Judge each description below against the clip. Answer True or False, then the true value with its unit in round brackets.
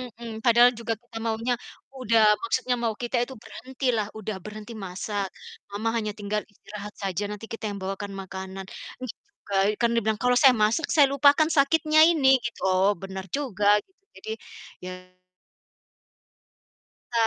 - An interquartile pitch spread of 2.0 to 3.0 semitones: False (3.5 semitones)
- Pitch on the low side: False (225 Hz)